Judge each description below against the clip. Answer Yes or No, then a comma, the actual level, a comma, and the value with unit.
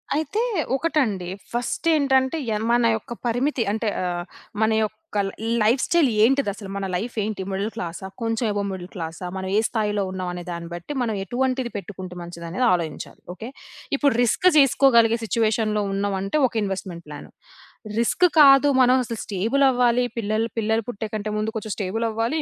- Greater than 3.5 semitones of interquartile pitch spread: Yes, average, 4.2 semitones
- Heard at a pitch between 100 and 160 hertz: No, high, 220 Hz